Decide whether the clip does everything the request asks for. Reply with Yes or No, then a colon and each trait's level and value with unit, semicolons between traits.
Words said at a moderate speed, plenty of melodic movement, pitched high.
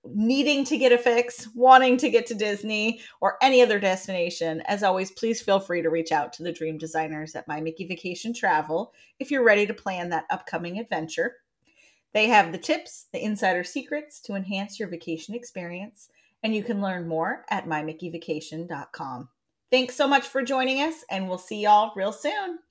Yes: average, 185 wpm; wide, 6.2 semitones; high, 205 Hz